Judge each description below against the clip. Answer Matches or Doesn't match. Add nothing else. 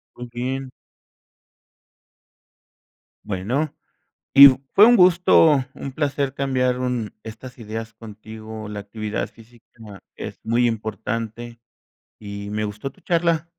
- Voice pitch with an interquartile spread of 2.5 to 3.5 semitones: Doesn't match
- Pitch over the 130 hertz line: Doesn't match